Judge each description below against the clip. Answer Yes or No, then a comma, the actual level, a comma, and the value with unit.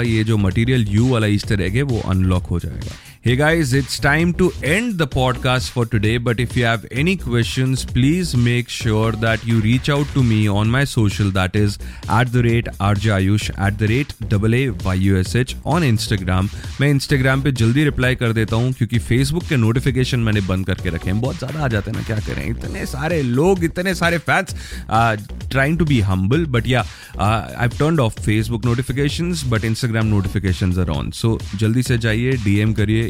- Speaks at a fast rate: Yes, fast, 200 wpm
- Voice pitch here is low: Yes, low, 115 Hz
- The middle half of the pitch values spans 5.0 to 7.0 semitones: No, average, 4.0 semitones